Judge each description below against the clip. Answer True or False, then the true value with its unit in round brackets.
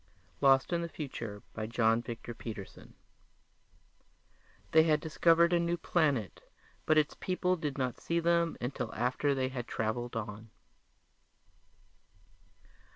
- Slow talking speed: True (130 wpm)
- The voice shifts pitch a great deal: True (6.2 semitones)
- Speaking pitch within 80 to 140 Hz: True (135 Hz)